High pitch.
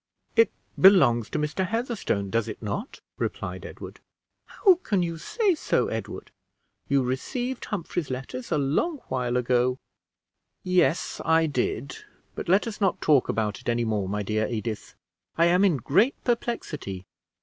No: medium, 145 Hz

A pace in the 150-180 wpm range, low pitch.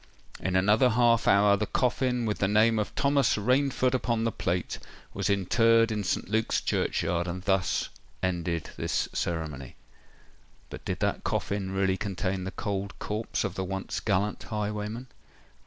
Yes: average, 155 wpm; low, 105 Hz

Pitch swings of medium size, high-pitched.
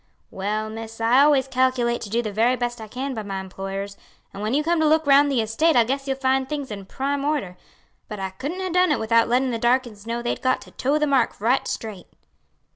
Yes: average, 4.1 semitones; high, 245 Hz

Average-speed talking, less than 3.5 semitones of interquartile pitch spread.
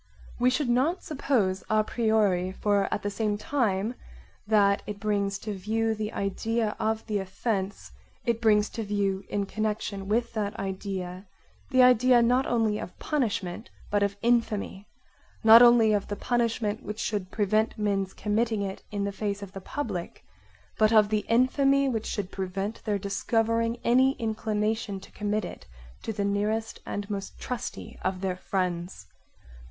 Yes: average, 160 wpm; narrow, 2.4 semitones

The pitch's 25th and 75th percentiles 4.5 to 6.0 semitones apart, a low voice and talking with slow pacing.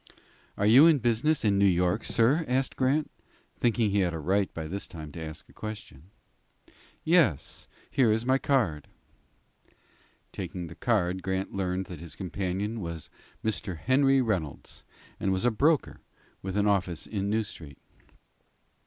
No: average, 5.3 semitones; low, 100 Hz; average, 155 wpm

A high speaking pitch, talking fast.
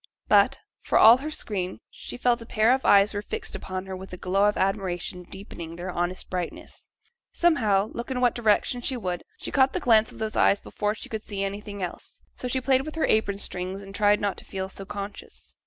Yes: high, 205 Hz; fast, 220 wpm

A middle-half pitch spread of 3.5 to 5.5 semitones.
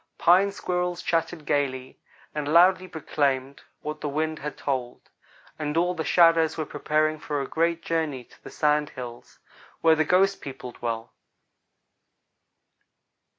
No: average, 3.1 semitones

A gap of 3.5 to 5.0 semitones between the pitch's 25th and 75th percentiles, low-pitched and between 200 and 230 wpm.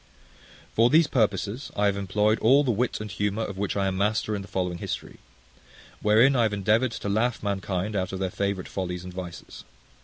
No: narrow, 2.5 semitones; low, 100 Hz; fast, 205 wpm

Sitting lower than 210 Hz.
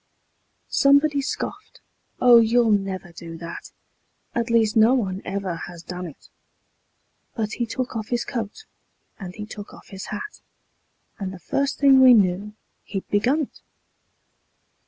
No: high, 215 Hz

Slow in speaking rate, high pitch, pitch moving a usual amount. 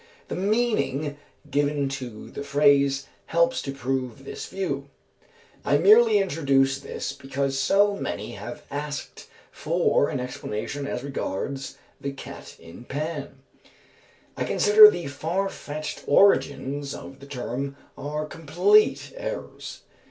No: slow, 120 wpm; medium, 140 Hz; average, 3.6 semitones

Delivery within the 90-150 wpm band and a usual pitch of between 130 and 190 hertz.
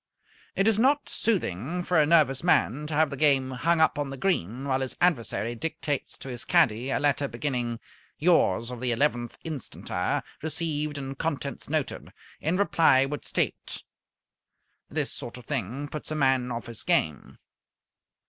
No: average, 165 wpm; medium, 140 Hz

